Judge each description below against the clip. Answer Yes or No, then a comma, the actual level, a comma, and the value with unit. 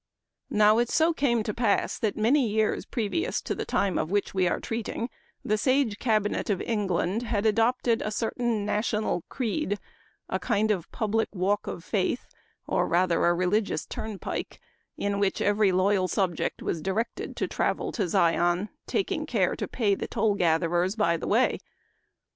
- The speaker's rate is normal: Yes, average, 170 wpm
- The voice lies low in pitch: No, high, 210 Hz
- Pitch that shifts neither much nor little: Yes, average, 3.3 semitones